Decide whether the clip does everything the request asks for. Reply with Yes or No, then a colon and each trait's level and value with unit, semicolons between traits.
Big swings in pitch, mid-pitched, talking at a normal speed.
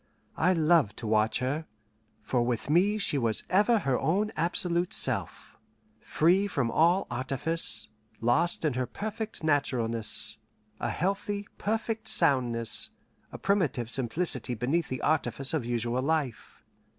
No: wide, 6.8 semitones; medium, 150 Hz; slow, 130 wpm